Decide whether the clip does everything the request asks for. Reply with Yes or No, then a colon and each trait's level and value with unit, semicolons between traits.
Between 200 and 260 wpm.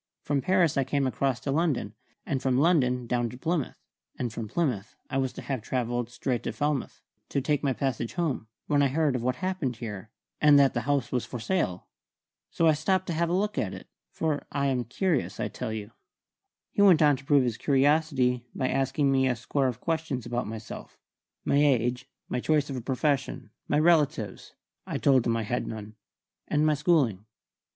Yes: fast, 205 wpm